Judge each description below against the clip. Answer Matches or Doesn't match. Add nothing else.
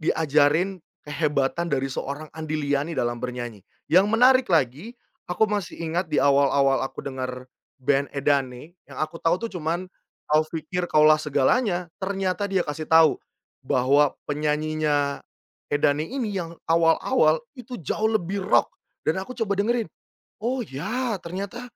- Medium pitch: Matches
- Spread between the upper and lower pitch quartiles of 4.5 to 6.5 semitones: Matches